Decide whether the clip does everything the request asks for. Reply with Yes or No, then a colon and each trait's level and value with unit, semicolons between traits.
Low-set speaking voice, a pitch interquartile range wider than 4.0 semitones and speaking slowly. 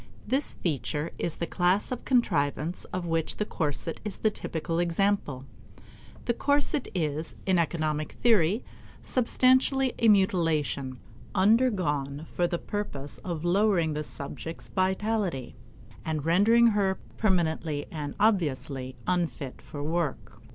No: medium, 175 Hz; wide, 5.4 semitones; slow, 125 wpm